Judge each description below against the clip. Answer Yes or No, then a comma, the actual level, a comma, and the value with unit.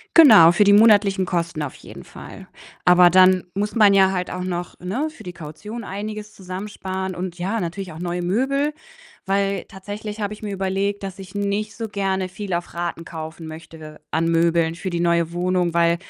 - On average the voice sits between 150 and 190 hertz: Yes, medium, 185 Hz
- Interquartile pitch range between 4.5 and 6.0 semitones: No, average, 2.8 semitones